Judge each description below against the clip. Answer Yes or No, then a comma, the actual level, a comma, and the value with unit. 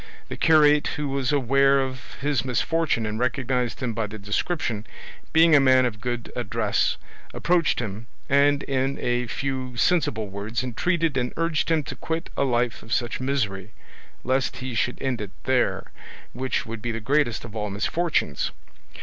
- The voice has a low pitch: Yes, low, 130 Hz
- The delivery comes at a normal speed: Yes, average, 165 wpm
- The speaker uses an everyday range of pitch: Yes, average, 3.6 semitones